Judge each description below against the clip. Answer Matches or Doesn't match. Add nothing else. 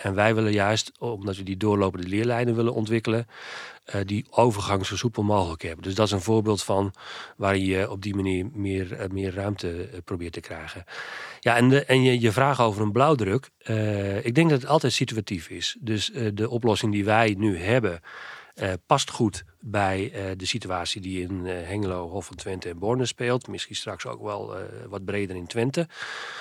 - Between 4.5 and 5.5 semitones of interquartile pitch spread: Doesn't match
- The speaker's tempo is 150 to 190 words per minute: Doesn't match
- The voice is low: Matches